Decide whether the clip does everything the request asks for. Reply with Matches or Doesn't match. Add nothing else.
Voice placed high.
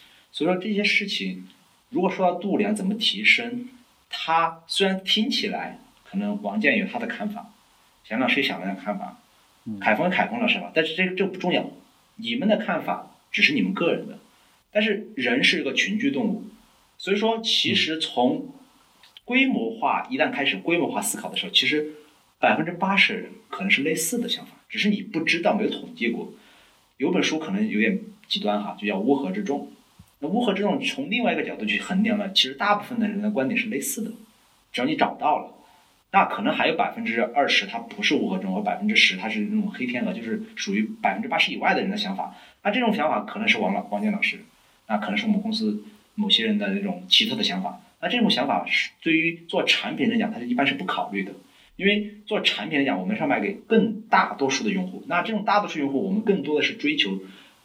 Matches